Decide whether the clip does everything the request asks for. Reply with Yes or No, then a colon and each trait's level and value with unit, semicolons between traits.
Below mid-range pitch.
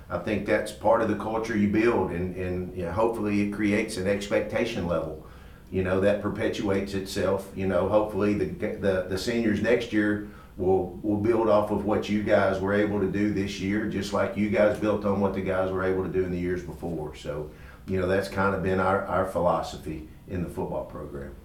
Yes: low, 100 Hz